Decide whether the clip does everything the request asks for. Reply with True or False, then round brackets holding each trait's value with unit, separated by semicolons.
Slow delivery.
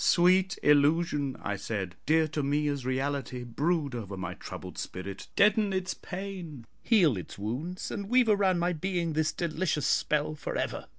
False (165 wpm)